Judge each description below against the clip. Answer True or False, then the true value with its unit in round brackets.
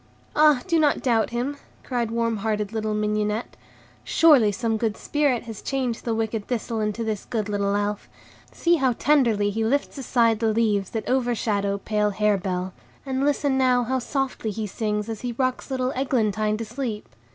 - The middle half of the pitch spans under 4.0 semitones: True (3.3 semitones)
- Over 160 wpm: True (175 wpm)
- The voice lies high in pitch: True (225 Hz)